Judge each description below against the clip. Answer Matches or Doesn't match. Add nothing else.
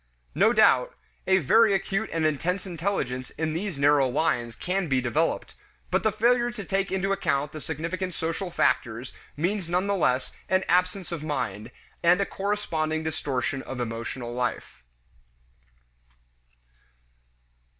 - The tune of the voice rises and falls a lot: Matches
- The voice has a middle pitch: Matches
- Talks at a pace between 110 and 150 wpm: Matches